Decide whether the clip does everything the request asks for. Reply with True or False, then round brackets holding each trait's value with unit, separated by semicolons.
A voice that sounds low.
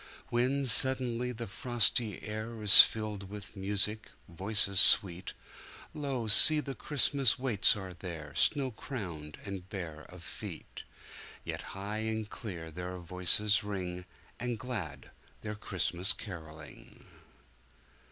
True (105 Hz)